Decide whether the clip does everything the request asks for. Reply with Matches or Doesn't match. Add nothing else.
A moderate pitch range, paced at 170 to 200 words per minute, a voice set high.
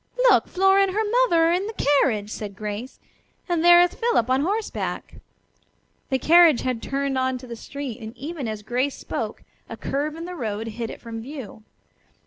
Doesn't match